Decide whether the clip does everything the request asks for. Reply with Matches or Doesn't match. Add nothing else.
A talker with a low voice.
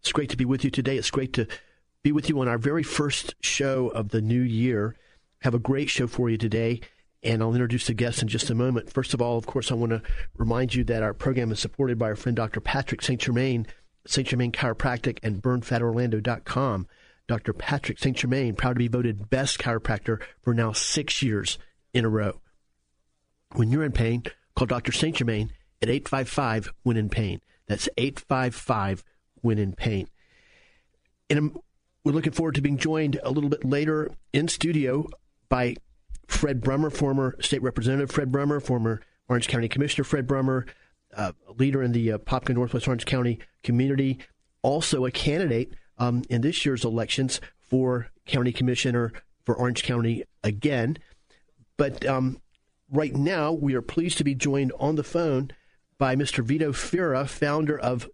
Matches